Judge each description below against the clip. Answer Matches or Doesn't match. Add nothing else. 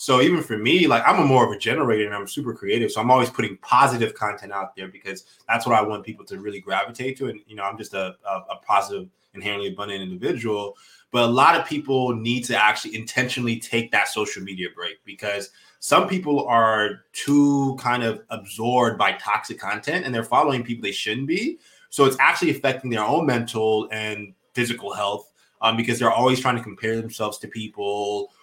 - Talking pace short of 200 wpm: Doesn't match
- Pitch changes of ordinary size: Matches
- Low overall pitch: Matches